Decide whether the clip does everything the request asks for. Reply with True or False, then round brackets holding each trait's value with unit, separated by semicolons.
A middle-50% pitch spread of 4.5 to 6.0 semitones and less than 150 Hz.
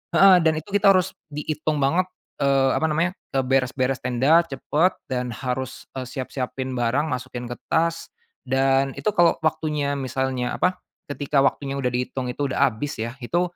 False (3.5 semitones; 135 Hz)